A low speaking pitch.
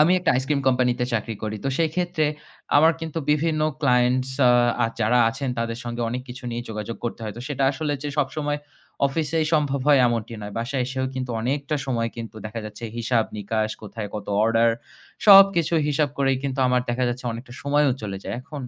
Yes: low, 130 Hz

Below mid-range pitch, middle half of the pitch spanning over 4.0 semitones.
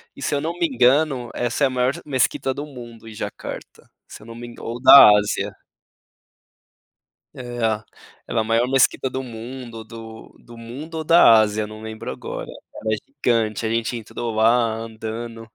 No: low, 120 Hz; average, 2.8 semitones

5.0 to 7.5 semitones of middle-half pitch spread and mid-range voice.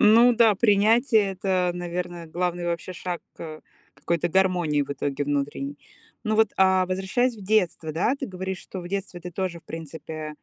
No: average, 3.2 semitones; medium, 180 Hz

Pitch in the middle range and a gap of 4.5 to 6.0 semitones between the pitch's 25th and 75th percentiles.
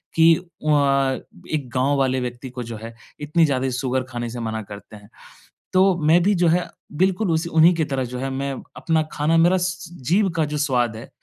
Yes: medium, 145 Hz; average, 4.8 semitones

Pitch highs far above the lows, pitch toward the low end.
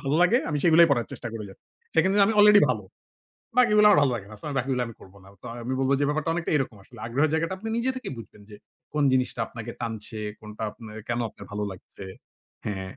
Yes: wide, 7.1 semitones; low, 130 Hz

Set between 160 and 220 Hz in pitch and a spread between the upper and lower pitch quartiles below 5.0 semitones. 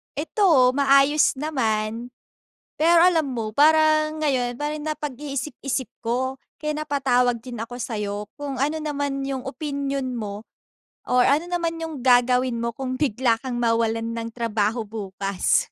No: very high, 260 Hz; average, 4.3 semitones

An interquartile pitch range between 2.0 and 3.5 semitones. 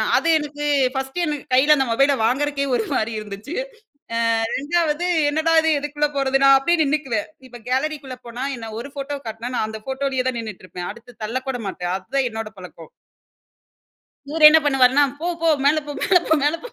No: average, 4.1 semitones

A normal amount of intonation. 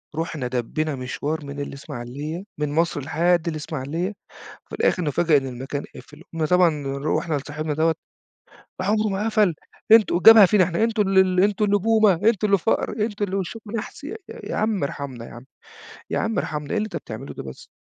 No: wide, 6.1 semitones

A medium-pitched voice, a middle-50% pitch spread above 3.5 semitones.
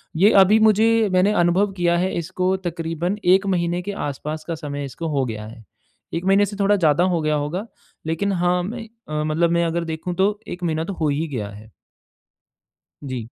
Yes: medium, 170 Hz; average, 3.9 semitones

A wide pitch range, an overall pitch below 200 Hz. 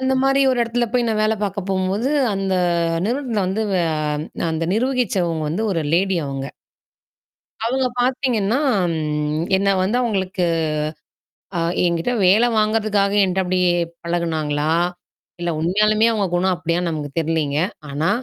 No: average, 4.8 semitones; high, 190 Hz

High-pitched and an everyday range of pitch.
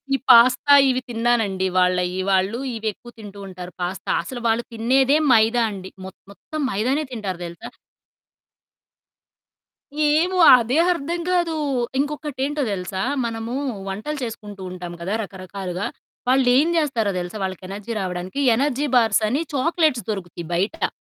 No: high, 225 Hz; wide, 6.0 semitones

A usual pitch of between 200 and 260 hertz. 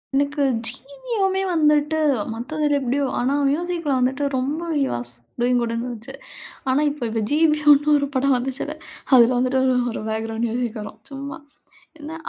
No: very high, 275 Hz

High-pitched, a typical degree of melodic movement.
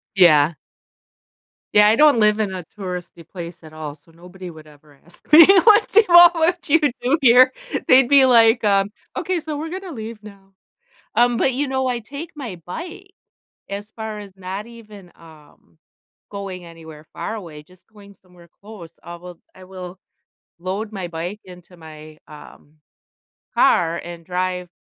No: high, 195 Hz; wide, 6.0 semitones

